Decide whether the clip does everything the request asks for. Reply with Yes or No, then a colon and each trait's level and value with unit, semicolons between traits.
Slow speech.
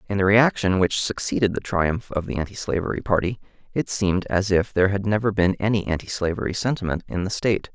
No: average, 195 wpm